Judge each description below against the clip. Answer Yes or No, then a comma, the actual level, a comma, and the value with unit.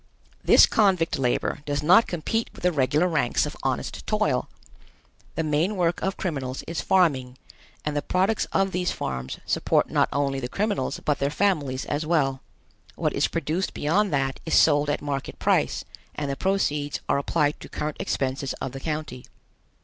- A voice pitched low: No, medium, 150 Hz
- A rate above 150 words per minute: Yes, average, 170 wpm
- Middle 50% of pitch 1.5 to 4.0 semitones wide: No, average, 4.7 semitones